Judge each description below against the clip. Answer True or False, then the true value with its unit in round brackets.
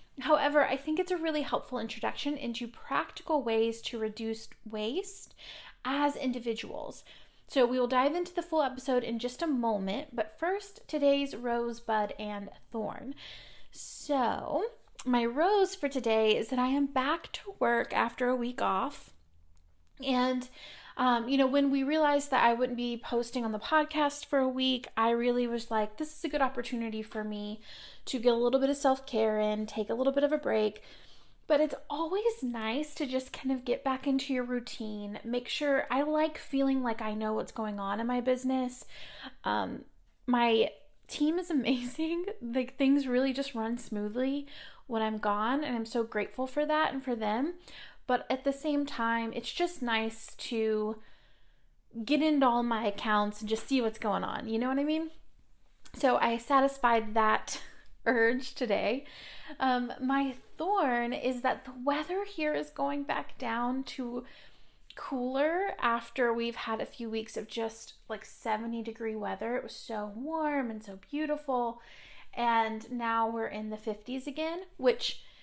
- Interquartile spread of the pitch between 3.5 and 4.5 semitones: True (4.0 semitones)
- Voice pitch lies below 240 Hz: False (250 Hz)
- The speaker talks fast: False (170 wpm)